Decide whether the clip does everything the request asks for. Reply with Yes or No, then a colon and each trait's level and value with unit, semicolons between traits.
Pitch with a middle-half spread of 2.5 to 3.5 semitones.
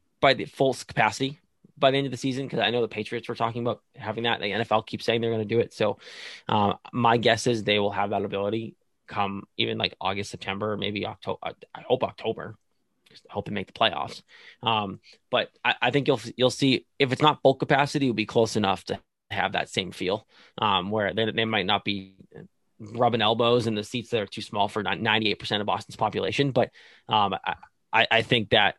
Yes: average, 3.0 semitones